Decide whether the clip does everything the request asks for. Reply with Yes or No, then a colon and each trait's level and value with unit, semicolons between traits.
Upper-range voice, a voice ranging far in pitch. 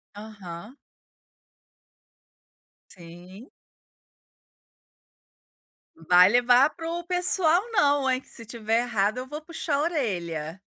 Yes: high, 240 Hz; wide, 7.9 semitones